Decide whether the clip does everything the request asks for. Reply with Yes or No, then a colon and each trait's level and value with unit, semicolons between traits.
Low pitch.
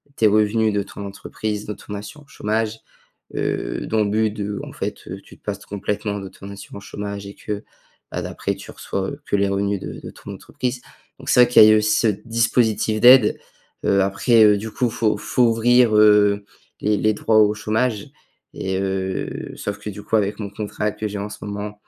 Yes: low, 105 Hz